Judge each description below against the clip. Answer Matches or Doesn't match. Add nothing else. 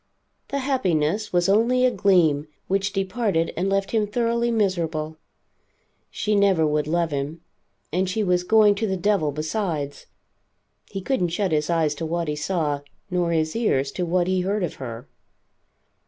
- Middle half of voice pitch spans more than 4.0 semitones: Matches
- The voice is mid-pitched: Matches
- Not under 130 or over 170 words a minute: Matches